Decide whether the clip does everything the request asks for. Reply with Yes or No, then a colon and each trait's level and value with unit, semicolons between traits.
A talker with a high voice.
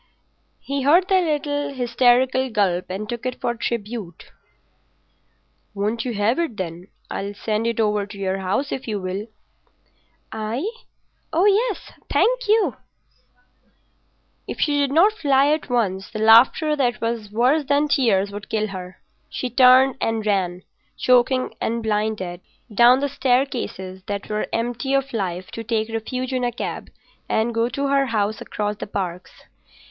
Yes: high, 230 Hz